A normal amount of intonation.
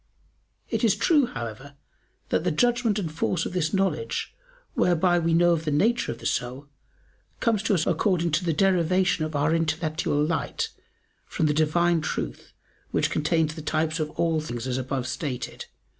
Yes: average, 3.1 semitones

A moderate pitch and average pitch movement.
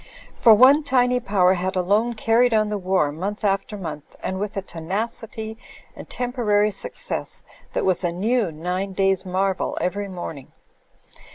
No: high, 200 Hz; average, 3.3 semitones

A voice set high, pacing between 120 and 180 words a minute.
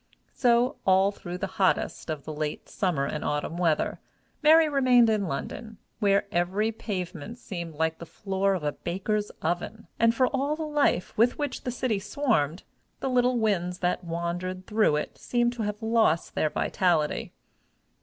Yes: high, 195 Hz; average, 165 wpm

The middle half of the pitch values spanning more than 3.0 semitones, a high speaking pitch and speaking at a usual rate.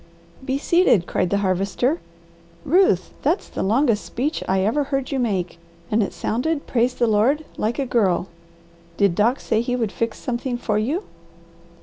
Yes: average, 5.1 semitones; high, 235 Hz; average, 165 wpm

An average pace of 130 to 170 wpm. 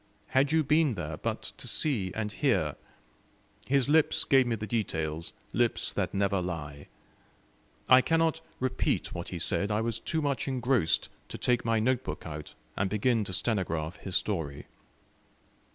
Yes: average, 160 wpm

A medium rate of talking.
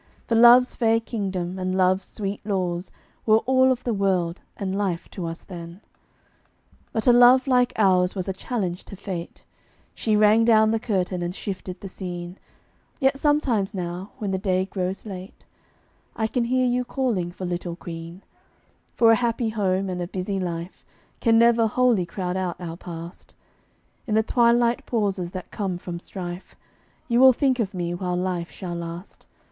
Yes: average, 175 wpm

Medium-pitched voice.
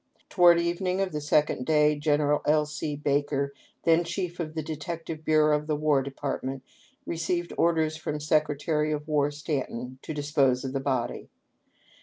Yes: medium, 150 Hz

